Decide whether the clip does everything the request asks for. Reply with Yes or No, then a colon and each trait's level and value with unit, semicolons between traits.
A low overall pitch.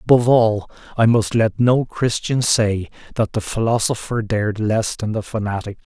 Yes: low, 110 Hz